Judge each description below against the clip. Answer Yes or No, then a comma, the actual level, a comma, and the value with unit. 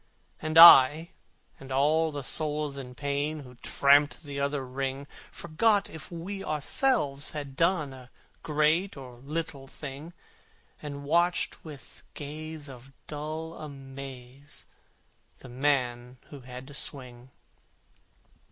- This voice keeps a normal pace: No, slow, 120 wpm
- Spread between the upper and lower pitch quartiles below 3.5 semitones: Yes, average, 2.7 semitones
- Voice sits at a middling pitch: Yes, medium, 145 Hz